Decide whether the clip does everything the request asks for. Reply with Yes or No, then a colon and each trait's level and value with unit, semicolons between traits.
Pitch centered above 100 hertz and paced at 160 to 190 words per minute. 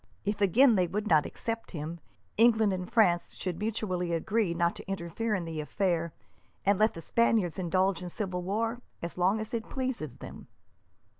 Yes: high, 190 Hz; average, 175 wpm